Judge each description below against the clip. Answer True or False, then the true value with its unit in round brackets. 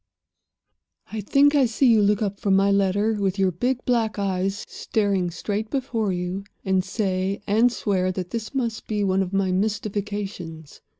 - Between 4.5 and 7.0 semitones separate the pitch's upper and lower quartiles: False (2.5 semitones)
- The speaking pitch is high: True (200 Hz)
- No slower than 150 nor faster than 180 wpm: True (170 wpm)